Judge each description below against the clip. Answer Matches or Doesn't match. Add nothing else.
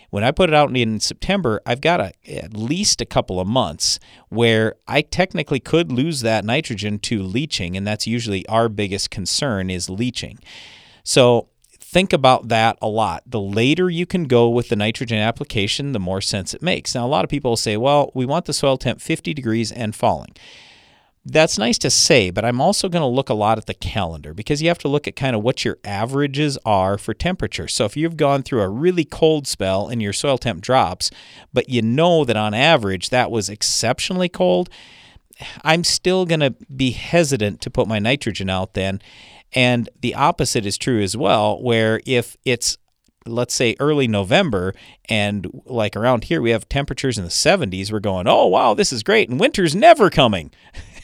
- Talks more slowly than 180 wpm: Doesn't match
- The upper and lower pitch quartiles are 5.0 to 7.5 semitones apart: Matches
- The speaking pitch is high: Doesn't match